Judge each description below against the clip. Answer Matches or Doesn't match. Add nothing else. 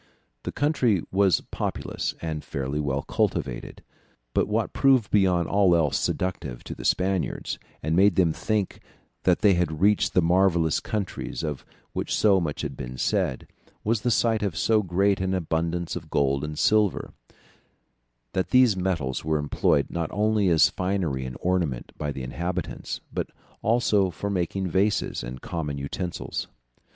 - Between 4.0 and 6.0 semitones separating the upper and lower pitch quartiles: Matches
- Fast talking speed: Doesn't match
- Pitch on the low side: Matches